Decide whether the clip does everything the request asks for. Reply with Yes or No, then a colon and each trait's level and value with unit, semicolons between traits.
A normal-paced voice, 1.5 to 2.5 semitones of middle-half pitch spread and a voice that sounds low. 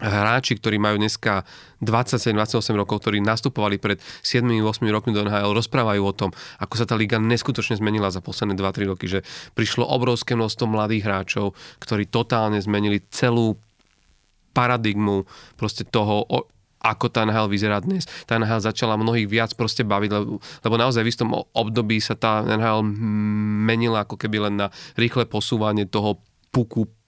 Yes: average, 155 wpm; narrow, 2.0 semitones; low, 110 Hz